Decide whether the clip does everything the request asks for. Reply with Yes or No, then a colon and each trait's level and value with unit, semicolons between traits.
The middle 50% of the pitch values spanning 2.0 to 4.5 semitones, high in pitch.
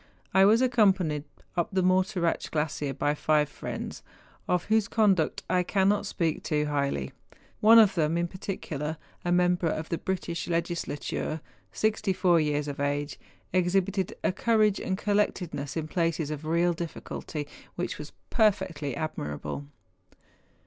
No: average, 4.0 semitones; medium, 170 Hz